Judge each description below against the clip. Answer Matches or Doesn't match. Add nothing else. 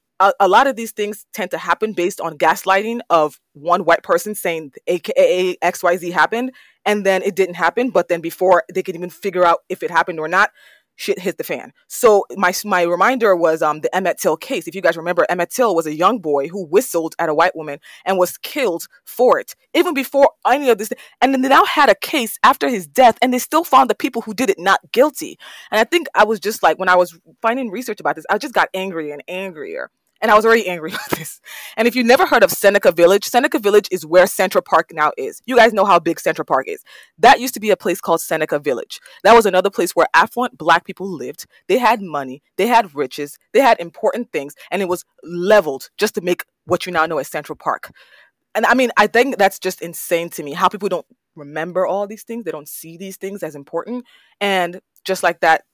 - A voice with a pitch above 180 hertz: Matches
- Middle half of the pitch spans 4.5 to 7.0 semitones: Matches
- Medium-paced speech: Doesn't match